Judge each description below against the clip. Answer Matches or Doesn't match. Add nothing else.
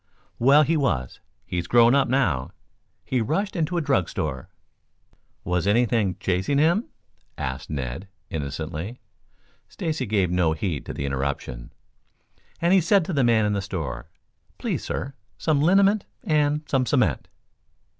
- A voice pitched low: Matches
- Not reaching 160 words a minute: Matches